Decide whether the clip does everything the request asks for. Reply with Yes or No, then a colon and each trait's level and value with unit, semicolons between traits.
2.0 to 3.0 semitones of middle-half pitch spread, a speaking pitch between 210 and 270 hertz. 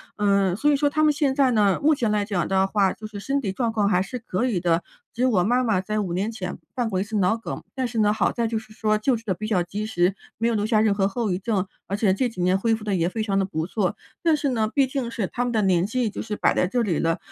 No: average, 3.6 semitones; high, 215 Hz